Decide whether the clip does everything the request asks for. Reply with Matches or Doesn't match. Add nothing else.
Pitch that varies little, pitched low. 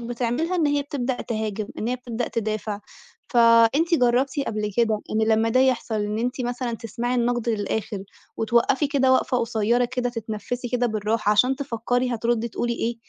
Doesn't match